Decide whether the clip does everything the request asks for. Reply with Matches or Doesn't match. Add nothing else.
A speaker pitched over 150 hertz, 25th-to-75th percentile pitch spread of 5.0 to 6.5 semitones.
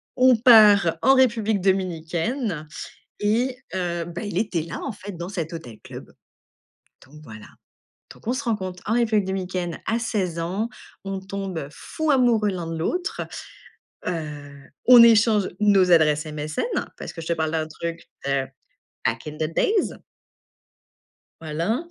Matches